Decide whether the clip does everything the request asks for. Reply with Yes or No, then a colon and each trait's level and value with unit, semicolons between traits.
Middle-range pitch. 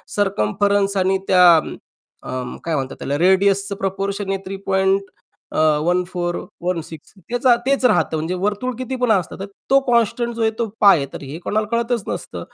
No: high, 195 Hz